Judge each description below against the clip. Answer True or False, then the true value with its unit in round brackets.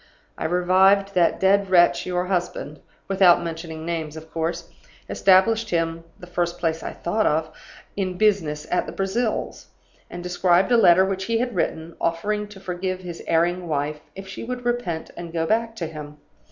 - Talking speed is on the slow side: False (175 wpm)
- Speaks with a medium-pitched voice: True (180 Hz)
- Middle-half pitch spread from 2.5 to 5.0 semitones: True (2.8 semitones)